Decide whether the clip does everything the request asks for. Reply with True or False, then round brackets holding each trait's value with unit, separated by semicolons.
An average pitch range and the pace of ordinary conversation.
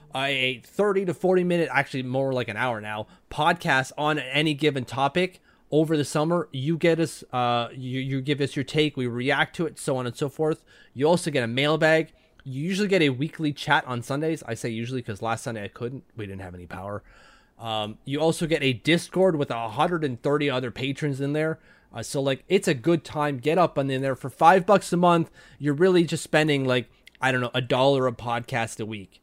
False (4.1 semitones; 220 wpm)